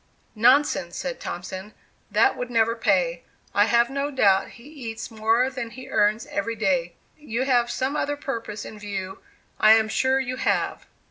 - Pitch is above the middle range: Yes, high, 230 Hz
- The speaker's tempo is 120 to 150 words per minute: No, average, 165 wpm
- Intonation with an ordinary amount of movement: Yes, average, 3.6 semitones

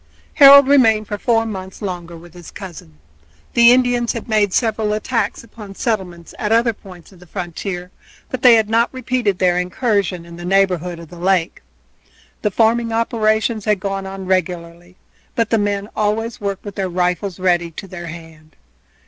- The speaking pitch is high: Yes, high, 195 Hz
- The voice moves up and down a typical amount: Yes, average, 4.1 semitones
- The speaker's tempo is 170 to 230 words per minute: Yes, average, 175 wpm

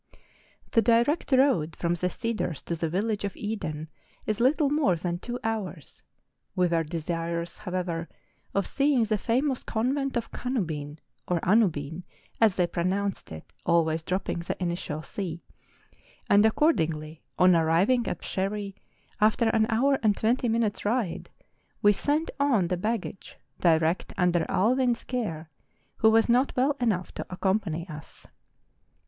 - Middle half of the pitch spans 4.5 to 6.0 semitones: Yes, wide, 5.4 semitones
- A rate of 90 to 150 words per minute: Yes, average, 145 wpm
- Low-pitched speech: No, high, 195 Hz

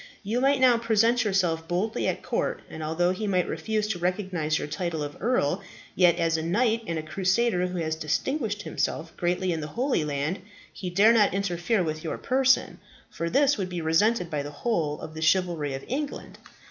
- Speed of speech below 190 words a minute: No, average, 195 wpm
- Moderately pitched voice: Yes, medium, 180 Hz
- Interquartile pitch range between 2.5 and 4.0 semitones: No, wide, 5.5 semitones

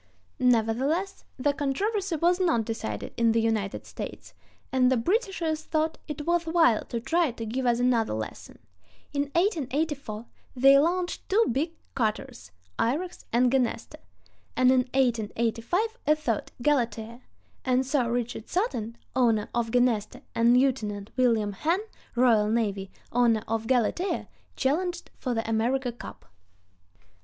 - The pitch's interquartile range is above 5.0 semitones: Yes, wide, 5.4 semitones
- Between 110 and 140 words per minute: Yes, slow, 135 wpm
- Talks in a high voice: Yes, very high, 250 Hz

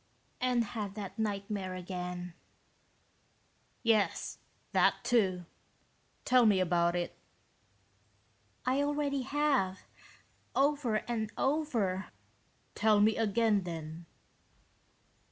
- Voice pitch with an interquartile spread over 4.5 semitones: Yes, average, 5.2 semitones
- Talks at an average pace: No, slow, 85 wpm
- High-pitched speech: Yes, high, 210 Hz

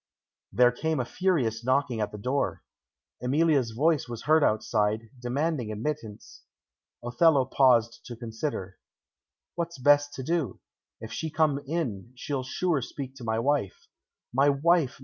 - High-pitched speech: No, low, 130 Hz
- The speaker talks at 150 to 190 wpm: No, average, 140 wpm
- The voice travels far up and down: No, average, 4.6 semitones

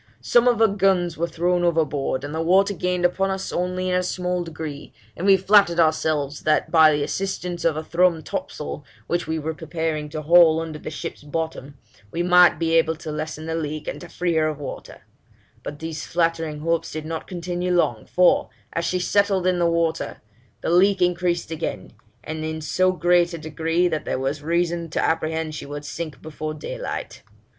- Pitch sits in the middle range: Yes, medium, 165 Hz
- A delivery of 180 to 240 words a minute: Yes, average, 195 wpm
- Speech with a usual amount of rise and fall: No, narrow, 2.2 semitones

